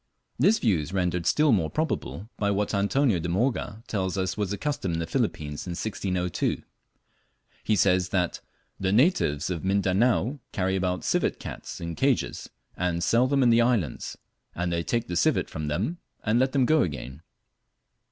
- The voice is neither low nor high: No, very low, 95 Hz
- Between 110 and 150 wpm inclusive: No, average, 175 wpm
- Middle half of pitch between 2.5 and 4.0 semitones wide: No, average, 5.2 semitones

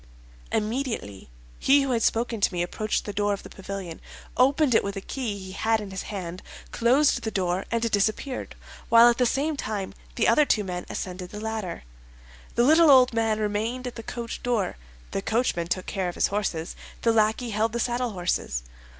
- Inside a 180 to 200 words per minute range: Yes, average, 195 wpm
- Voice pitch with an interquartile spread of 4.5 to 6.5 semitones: No, average, 3.8 semitones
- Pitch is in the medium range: No, high, 220 Hz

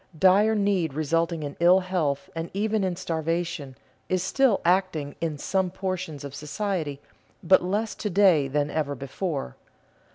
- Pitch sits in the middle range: Yes, medium, 170 Hz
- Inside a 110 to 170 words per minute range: Yes, average, 150 wpm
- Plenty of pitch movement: No, average, 4.3 semitones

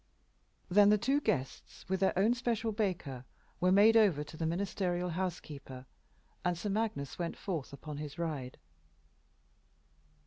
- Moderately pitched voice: Yes, medium, 180 Hz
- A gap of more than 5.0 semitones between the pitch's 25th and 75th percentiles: Yes, wide, 5.4 semitones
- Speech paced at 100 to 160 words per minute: Yes, average, 145 wpm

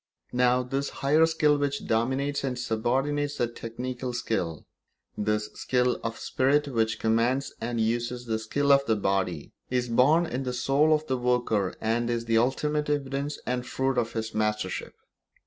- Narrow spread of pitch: No, average, 3.5 semitones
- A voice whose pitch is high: No, low, 125 Hz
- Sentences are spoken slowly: No, average, 165 wpm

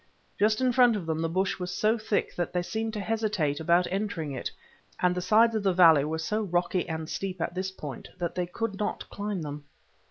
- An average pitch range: Yes, average, 4.4 semitones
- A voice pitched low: No, medium, 185 Hz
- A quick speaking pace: Yes, fast, 225 wpm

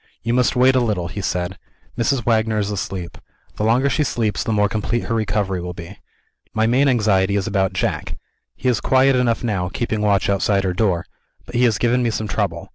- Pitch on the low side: Yes, low, 110 Hz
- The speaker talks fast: Yes, fast, 210 wpm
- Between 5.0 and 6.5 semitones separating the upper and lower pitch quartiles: No, average, 3.7 semitones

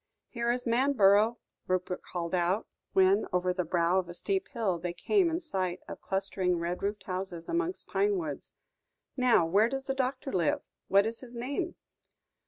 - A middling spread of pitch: No, wide, 6.5 semitones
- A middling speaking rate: Yes, average, 175 wpm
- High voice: Yes, high, 200 Hz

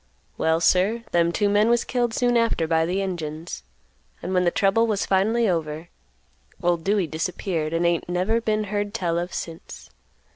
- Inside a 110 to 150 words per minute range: No, average, 175 wpm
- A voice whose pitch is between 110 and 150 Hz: No, medium, 185 Hz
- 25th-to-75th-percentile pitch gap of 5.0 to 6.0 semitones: No, average, 4.0 semitones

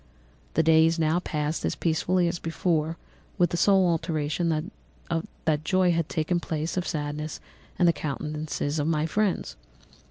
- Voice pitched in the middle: Yes, medium, 160 Hz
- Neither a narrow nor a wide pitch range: No, narrow, 2.2 semitones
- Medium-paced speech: Yes, average, 150 wpm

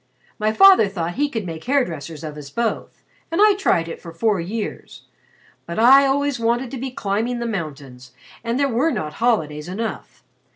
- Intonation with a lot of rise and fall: Yes, wide, 7.7 semitones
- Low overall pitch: No, high, 225 Hz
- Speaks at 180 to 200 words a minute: Yes, average, 190 wpm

